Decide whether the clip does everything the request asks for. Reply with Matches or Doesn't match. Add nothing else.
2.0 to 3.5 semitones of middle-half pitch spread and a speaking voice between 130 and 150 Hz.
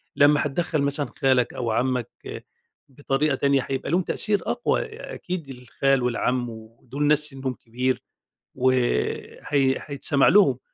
Matches